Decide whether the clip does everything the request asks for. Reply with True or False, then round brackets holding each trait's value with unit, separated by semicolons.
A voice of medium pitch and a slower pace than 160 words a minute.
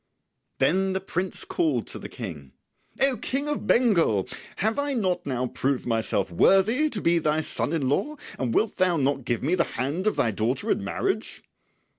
False (165 Hz; 185 wpm)